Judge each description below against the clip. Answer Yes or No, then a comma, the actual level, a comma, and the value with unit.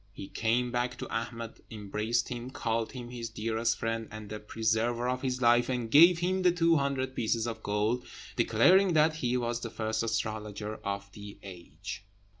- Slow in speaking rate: No, average, 180 wpm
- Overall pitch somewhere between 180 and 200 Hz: No, low, 115 Hz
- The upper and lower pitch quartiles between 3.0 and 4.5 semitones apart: No, narrow, 2.4 semitones